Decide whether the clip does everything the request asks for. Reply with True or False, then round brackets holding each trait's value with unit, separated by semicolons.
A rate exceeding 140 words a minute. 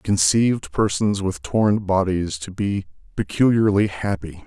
False (135 wpm)